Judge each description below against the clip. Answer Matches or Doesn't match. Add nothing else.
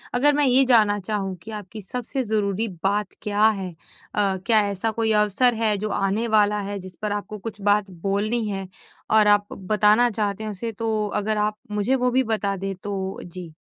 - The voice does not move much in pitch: Matches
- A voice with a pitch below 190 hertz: Doesn't match